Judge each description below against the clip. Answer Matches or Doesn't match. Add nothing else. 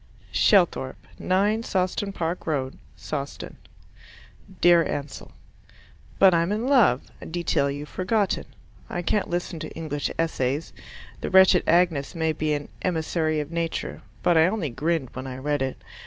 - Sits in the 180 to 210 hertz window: Doesn't match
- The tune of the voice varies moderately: Matches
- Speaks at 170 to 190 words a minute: Doesn't match